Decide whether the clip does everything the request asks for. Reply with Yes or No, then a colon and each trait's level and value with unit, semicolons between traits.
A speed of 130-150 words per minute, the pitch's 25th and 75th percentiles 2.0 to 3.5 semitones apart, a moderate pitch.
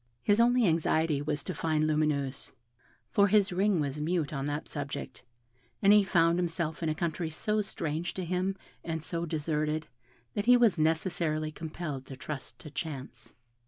No: average, 165 wpm; average, 3.1 semitones; medium, 160 Hz